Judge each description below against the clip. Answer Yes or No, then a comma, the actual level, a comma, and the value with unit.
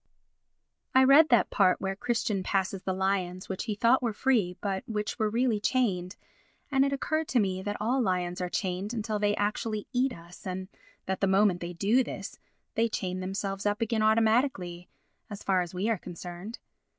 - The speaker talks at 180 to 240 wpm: Yes, average, 185 wpm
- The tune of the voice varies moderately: Yes, average, 3.7 semitones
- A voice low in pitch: No, high, 205 Hz